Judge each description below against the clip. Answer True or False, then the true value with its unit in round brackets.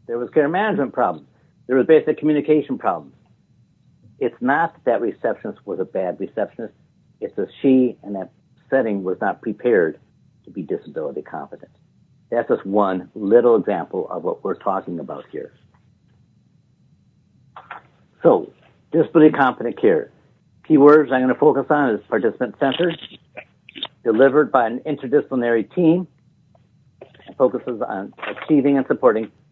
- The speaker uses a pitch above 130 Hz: True (140 Hz)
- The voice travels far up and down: False (3.8 semitones)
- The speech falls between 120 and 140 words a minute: True (135 wpm)